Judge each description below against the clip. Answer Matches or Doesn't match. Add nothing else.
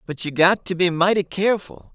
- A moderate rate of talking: Doesn't match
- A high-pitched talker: Doesn't match